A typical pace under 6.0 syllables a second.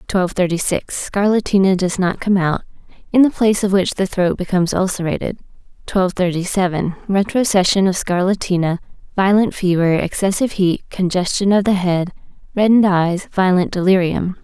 Yes: 5.5 syllables/s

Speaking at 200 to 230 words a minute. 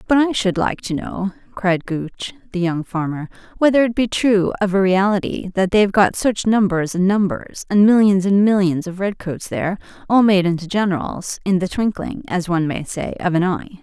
Yes: fast, 205 wpm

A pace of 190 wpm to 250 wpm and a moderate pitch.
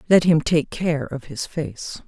Yes: fast, 205 wpm; medium, 155 Hz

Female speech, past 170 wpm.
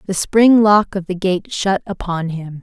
Yes: female; fast, 205 wpm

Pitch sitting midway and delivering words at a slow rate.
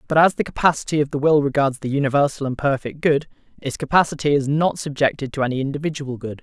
No: medium, 145 Hz; fast, 205 wpm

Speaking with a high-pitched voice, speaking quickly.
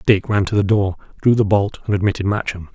No: low, 100 Hz; fast, 240 wpm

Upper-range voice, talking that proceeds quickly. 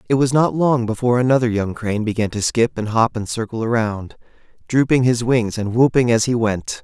No: low, 115 Hz; fast, 210 wpm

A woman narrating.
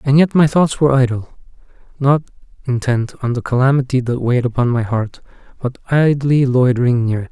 No: male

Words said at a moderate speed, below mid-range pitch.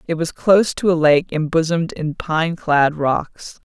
No: average, 180 wpm; medium, 160 Hz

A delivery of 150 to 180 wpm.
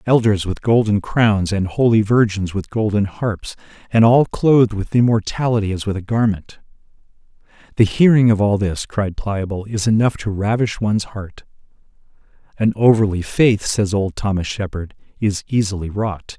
Yes: average, 155 wpm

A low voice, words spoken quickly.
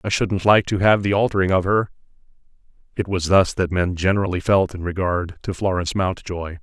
No: very low, 95 Hz; average, 190 wpm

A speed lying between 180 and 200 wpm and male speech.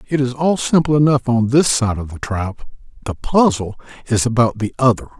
Yes: average, 195 wpm; male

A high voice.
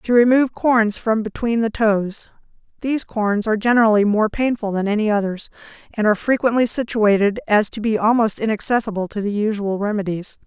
Yes: high, 215 Hz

